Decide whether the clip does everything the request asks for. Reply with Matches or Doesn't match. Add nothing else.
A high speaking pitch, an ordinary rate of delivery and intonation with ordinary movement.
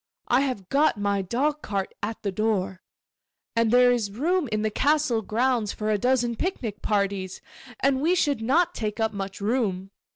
Matches